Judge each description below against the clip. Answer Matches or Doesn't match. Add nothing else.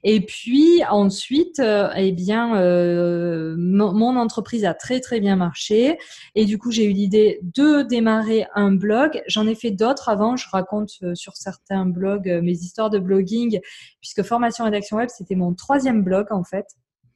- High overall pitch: Matches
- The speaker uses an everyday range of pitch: Matches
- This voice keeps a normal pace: Matches